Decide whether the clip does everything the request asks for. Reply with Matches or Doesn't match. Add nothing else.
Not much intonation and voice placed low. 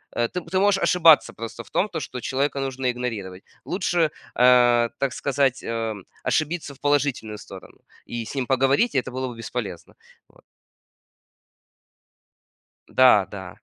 Doesn't match